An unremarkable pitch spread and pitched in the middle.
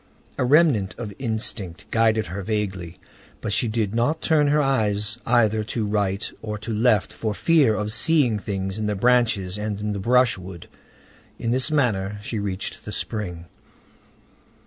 No: average, 3.1 semitones; low, 110 Hz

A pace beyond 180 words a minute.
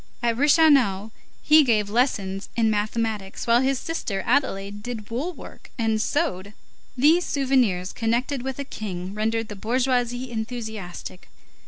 No: slow, 135 wpm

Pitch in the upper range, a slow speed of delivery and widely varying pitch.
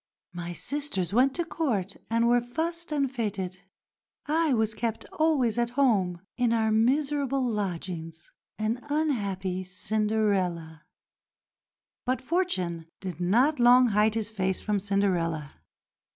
Yes: high, 220 Hz; slow, 125 wpm; wide, 5.7 semitones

